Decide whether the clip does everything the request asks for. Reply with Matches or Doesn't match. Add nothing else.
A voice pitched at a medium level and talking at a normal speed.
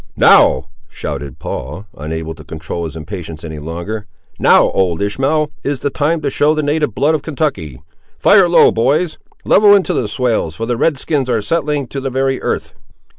Doesn't match